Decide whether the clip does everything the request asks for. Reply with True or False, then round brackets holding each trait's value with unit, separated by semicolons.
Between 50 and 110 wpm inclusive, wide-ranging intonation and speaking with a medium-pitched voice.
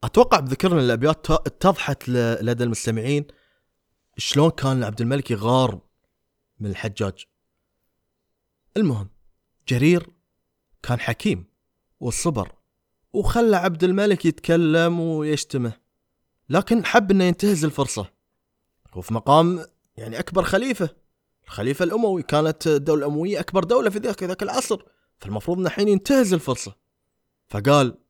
True (105 wpm; 7.7 semitones; 155 Hz)